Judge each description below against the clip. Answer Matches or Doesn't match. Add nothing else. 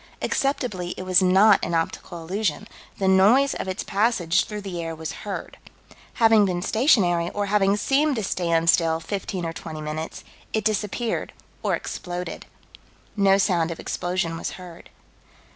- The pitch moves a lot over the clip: Doesn't match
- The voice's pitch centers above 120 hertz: Matches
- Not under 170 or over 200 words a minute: Doesn't match